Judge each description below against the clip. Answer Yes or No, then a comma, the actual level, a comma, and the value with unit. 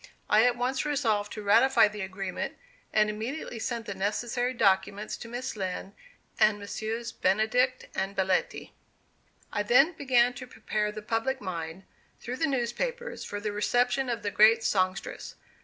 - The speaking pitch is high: Yes, high, 220 Hz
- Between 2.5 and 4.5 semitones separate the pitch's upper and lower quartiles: Yes, average, 3.3 semitones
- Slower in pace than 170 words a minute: Yes, average, 155 wpm